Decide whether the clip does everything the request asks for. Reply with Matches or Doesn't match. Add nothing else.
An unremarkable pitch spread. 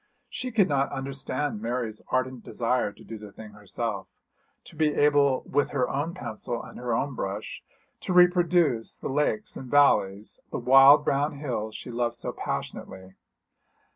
Matches